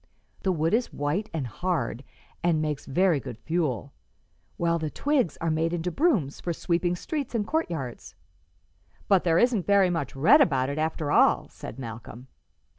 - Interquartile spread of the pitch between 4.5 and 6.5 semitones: Yes, average, 5.1 semitones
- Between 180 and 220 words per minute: No, average, 165 wpm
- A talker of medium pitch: Yes, medium, 165 Hz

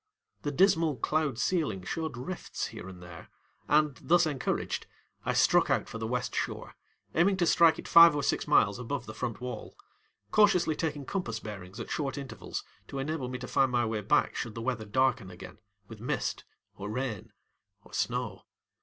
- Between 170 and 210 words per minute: Yes, average, 180 wpm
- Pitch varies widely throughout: Yes, wide, 5.9 semitones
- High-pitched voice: No, low, 130 Hz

